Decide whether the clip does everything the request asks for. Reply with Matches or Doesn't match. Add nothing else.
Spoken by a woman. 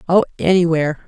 Matches